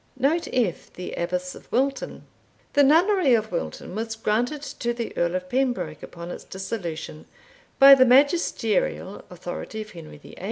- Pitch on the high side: Yes, high, 225 Hz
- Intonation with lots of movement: Yes, wide, 6.9 semitones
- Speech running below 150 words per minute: No, average, 155 wpm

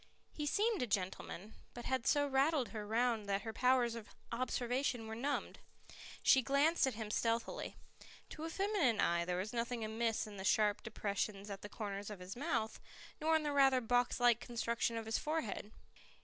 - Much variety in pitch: No, average, 4.1 semitones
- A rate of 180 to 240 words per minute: Yes, average, 185 wpm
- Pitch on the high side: Yes, high, 235 Hz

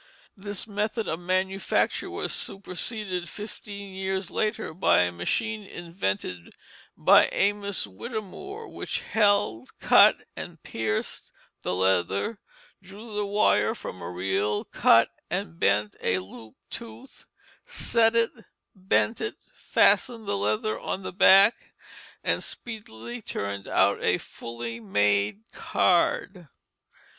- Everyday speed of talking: No, slow, 115 wpm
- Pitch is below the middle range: No, high, 190 Hz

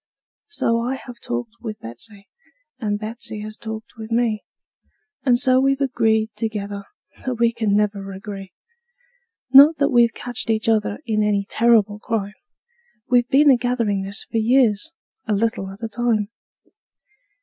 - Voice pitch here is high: Yes, high, 225 Hz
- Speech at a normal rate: Yes, average, 150 wpm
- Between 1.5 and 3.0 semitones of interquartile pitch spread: Yes, average, 2.7 semitones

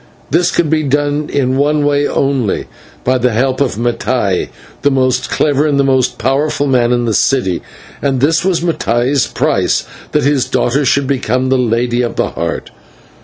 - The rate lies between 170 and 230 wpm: Yes, average, 175 wpm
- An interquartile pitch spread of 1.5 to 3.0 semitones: Yes, average, 2.7 semitones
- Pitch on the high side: No, low, 135 Hz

